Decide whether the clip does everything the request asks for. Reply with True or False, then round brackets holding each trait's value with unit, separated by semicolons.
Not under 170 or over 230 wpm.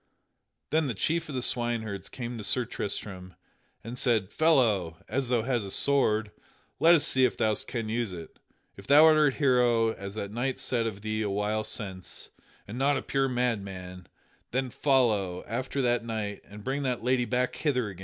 True (190 wpm)